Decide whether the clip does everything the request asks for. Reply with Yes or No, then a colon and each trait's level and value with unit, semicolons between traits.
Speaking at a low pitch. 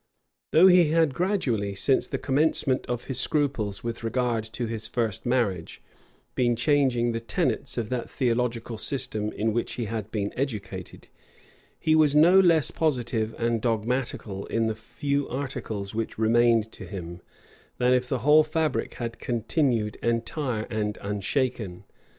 Yes: low, 120 Hz